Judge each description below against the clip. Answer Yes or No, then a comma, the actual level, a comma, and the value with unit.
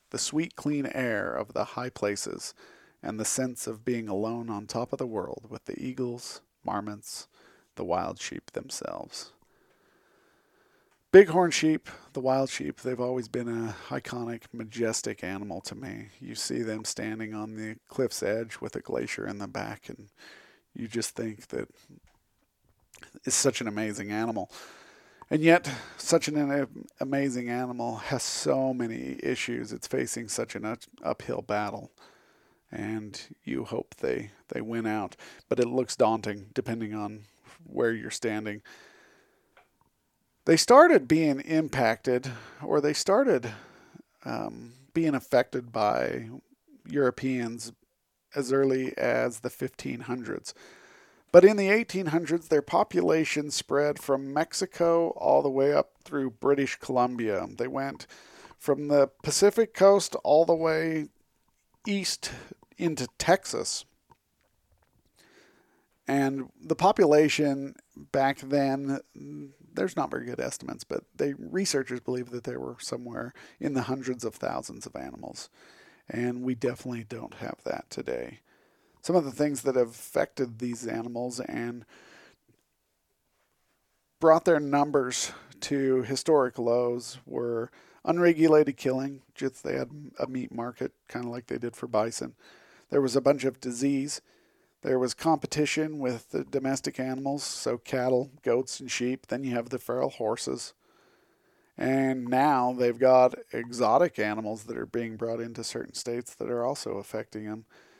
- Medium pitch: No, low, 130 Hz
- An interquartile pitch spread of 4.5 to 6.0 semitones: No, average, 3.9 semitones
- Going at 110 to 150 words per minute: Yes, average, 140 wpm